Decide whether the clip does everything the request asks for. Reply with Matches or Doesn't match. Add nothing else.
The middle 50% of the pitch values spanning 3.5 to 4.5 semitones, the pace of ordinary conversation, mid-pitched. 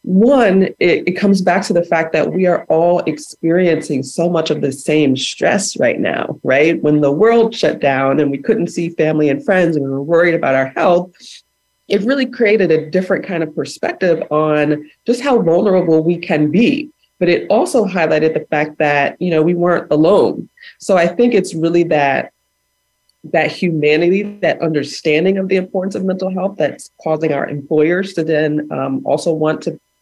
Matches